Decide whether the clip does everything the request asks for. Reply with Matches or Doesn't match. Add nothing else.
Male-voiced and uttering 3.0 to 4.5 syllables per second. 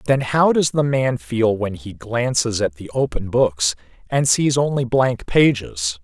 Matches